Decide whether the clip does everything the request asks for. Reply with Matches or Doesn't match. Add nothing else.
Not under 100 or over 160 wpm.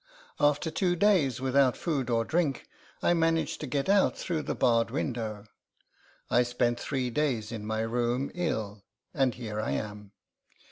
Matches